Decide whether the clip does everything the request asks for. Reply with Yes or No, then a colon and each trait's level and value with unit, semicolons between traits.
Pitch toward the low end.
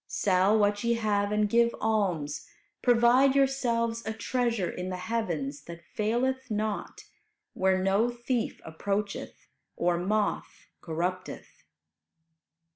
No: high, 210 Hz